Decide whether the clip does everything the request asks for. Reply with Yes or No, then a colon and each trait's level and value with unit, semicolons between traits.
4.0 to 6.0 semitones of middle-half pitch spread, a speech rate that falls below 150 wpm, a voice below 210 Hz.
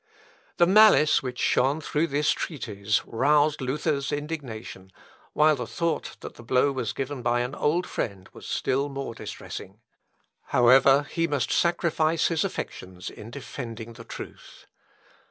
Yes: average, 4.3 semitones; average, 140 wpm; medium, 140 Hz